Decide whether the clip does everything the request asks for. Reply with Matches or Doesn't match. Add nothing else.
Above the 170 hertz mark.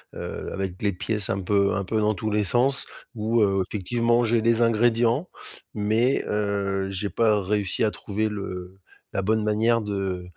Doesn't match